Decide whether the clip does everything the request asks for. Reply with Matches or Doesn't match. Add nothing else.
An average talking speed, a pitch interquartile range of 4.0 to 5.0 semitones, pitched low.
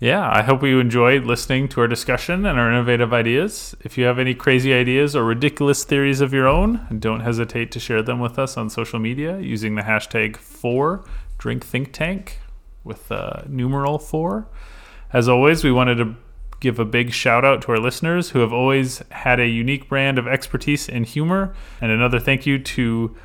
Doesn't match